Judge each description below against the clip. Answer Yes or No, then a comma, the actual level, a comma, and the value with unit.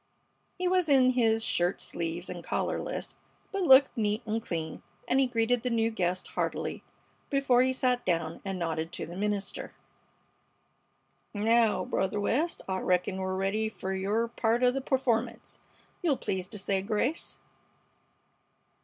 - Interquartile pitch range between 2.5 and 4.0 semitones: No, average, 4.8 semitones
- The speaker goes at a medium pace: Yes, average, 150 wpm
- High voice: Yes, high, 220 Hz